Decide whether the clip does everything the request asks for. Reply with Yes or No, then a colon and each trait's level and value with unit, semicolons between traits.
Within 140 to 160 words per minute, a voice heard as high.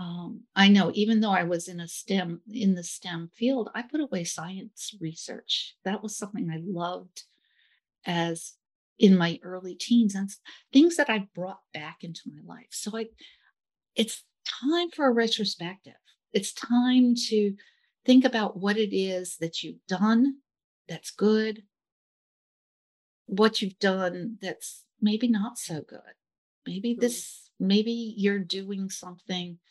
Yes: average, 145 wpm; high, 205 Hz